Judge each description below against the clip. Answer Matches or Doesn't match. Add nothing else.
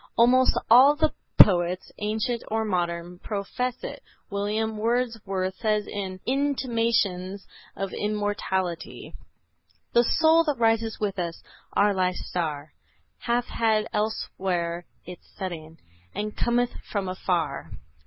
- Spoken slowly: Matches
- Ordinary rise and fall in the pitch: Matches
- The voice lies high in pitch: Matches